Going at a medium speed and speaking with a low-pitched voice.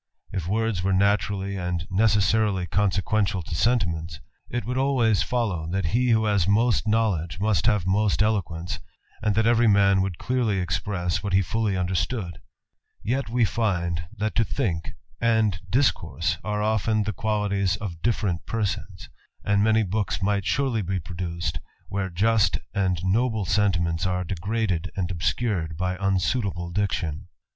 Yes: average, 150 wpm; low, 100 Hz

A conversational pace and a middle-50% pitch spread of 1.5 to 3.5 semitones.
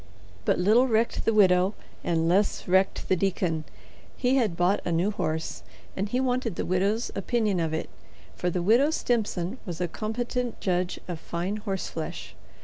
No: average, 165 wpm; average, 4.2 semitones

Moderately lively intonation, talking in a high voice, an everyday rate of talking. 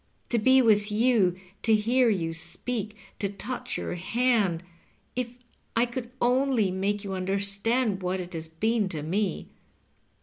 Yes: average, 4.3 semitones; high, 210 Hz; average, 155 wpm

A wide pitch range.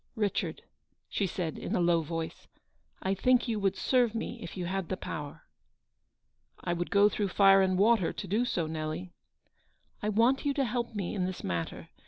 No: average, 4.3 semitones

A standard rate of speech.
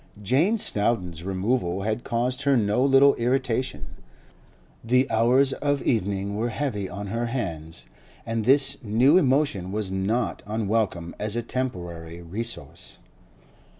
No: slow, 125 wpm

